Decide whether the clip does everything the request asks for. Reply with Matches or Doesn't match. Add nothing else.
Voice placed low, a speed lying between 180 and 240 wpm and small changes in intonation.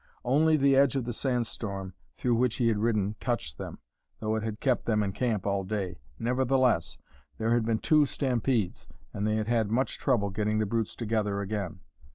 Doesn't match